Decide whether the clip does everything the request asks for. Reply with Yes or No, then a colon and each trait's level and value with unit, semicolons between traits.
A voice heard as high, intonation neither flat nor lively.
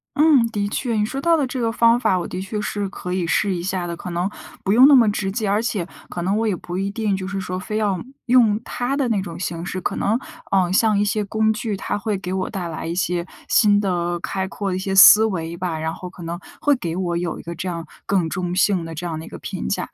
Yes: high, 195 Hz; average, 3.6 semitones